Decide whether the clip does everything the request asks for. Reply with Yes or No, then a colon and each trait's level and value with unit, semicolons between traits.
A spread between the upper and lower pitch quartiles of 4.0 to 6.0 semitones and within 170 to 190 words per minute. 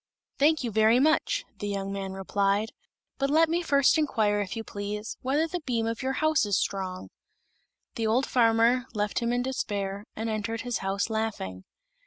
Yes: average, 4.4 semitones; average, 180 wpm